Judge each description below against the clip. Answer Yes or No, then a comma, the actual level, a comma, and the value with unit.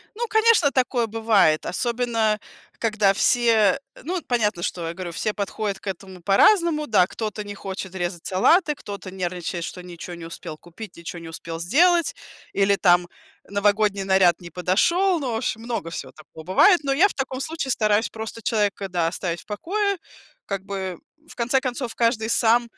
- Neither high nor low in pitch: No, high, 210 Hz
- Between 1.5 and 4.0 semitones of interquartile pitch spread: No, average, 5.2 semitones